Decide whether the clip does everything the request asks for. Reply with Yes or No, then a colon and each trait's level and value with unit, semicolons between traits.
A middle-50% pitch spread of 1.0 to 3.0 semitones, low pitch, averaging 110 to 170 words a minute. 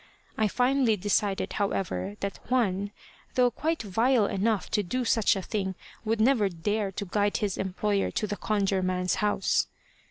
No: narrow, 2.6 semitones; high, 205 Hz; average, 160 wpm